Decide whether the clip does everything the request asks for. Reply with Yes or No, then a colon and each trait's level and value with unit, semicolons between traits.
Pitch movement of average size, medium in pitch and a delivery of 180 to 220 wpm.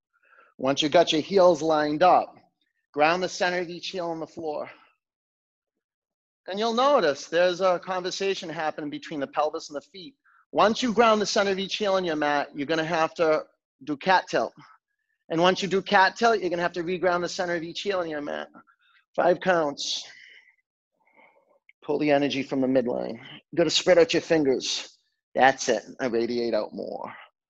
Yes: average, 4.1 semitones; medium, 175 Hz; average, 190 wpm